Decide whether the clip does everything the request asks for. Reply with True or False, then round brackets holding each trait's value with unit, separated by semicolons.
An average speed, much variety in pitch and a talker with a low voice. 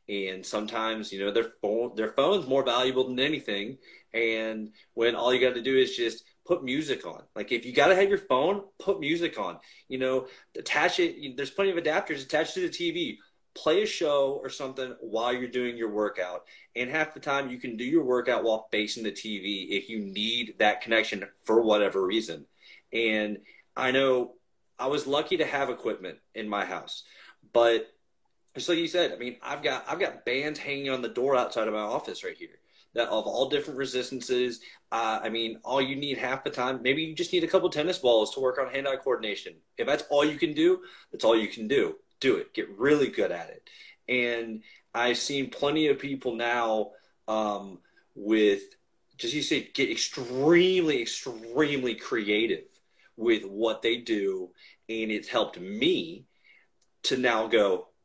True (190 wpm; 8.0 semitones; 130 Hz)